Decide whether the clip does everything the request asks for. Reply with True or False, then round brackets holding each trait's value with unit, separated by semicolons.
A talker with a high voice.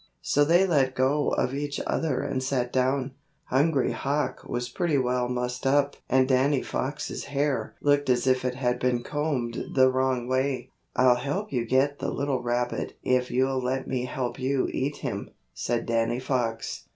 False (130 Hz)